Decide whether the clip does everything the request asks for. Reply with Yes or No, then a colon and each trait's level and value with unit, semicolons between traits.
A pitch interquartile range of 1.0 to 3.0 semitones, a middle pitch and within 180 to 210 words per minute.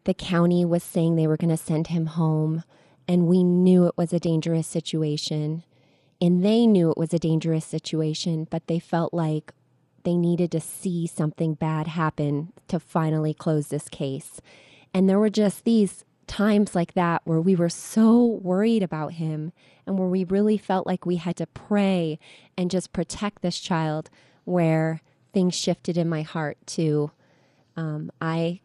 No: narrow, 2.4 semitones; medium, 165 Hz; average, 170 wpm